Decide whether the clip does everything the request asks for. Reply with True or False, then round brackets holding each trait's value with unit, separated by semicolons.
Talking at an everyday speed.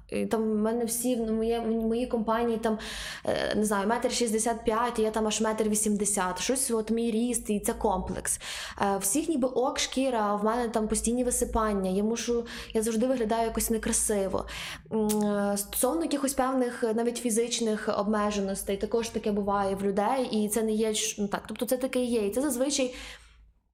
False (165 wpm)